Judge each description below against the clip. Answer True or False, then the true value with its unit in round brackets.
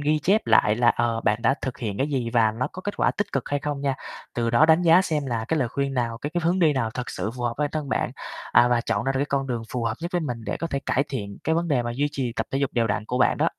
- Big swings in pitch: False (4.2 semitones)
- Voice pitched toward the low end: True (130 Hz)